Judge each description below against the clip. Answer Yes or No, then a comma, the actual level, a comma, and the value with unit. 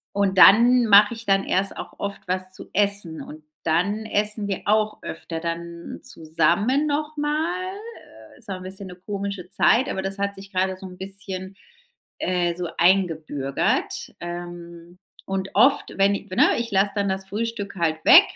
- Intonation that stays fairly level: No, average, 3.0 semitones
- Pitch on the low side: No, high, 195 Hz